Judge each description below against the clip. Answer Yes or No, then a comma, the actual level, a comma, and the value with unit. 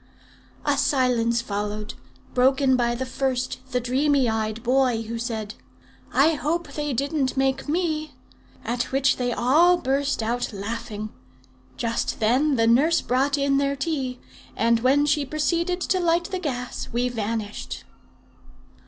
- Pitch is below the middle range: No, very high, 260 Hz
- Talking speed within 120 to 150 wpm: Yes, average, 140 wpm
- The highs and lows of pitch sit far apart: No, average, 3.7 semitones